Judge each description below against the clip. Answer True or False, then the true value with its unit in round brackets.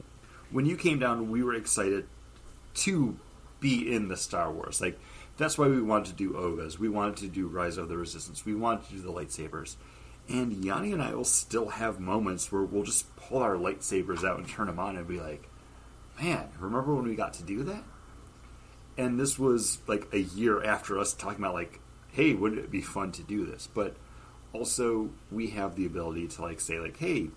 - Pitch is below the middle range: True (100 Hz)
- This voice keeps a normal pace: False (210 wpm)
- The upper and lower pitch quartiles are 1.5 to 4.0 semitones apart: False (4.6 semitones)